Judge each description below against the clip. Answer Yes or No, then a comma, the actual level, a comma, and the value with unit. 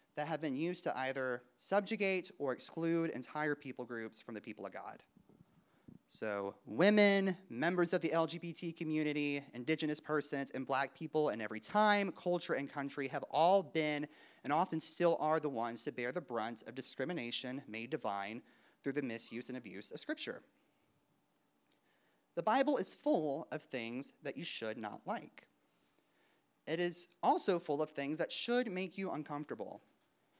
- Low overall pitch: No, medium, 150 Hz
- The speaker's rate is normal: Yes, average, 160 wpm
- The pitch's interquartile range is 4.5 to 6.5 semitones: Yes, average, 5.0 semitones